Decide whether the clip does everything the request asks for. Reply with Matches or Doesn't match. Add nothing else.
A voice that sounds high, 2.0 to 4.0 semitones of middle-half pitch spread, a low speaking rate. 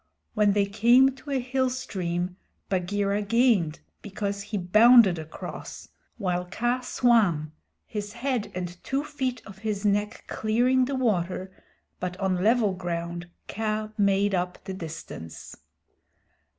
Doesn't match